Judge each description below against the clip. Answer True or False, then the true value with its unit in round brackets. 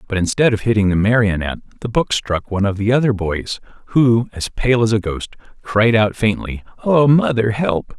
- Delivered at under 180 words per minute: False (195 wpm)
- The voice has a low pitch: True (110 Hz)